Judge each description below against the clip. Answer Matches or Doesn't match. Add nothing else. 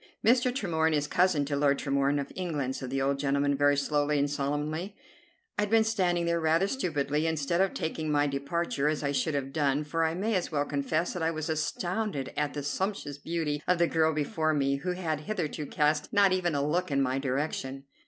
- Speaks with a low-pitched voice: Doesn't match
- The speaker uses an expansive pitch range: Doesn't match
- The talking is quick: Matches